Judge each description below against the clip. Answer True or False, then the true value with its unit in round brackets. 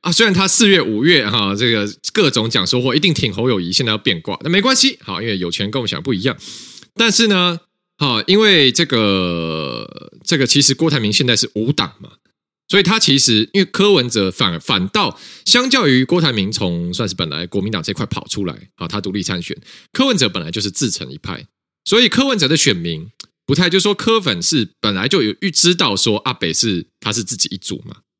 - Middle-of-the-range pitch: True (145 Hz)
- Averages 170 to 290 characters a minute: False (320 characters per minute)